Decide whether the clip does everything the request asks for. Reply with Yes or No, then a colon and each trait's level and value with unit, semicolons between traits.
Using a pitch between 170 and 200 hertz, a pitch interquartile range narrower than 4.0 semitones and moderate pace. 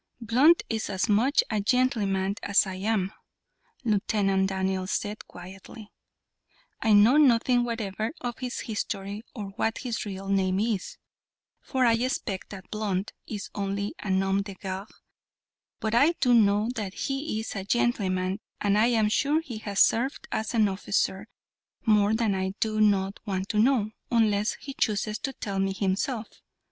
No: high, 210 Hz; average, 2.9 semitones; average, 160 wpm